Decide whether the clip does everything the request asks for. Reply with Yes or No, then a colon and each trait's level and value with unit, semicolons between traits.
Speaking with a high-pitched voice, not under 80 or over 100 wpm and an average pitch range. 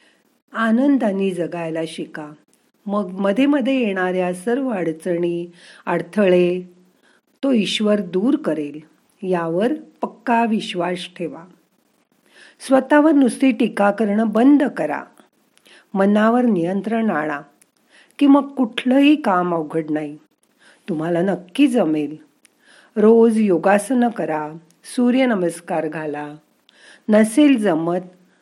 No: high, 200 Hz; average, 90 wpm; wide, 6.2 semitones